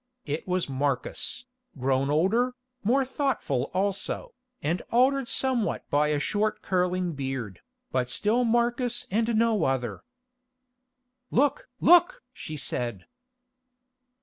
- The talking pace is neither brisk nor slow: No, slow, 110 wpm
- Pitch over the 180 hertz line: Yes, high, 190 Hz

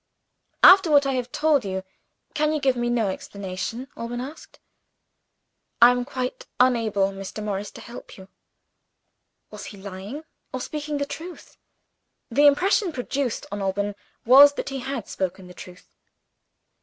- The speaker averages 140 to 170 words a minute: Yes, average, 150 wpm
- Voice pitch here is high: Yes, high, 245 Hz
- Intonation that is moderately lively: No, wide, 6.0 semitones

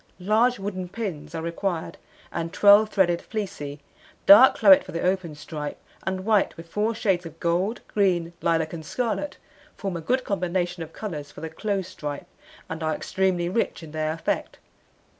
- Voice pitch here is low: No, medium, 180 Hz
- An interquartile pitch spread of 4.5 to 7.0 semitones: No, average, 3.9 semitones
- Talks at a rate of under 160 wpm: No, average, 170 wpm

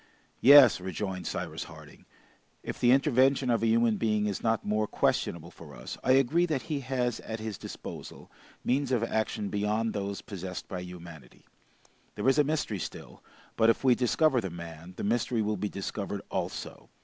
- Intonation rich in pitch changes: No, average, 4.4 semitones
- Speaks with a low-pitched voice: Yes, low, 110 Hz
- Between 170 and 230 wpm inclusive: Yes, average, 175 wpm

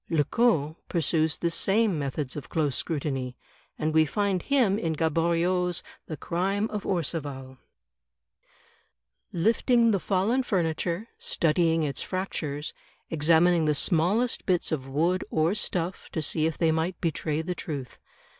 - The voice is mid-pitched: Yes, medium, 165 Hz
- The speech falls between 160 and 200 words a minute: No, slow, 135 wpm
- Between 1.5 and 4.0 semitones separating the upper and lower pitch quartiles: Yes, average, 3.3 semitones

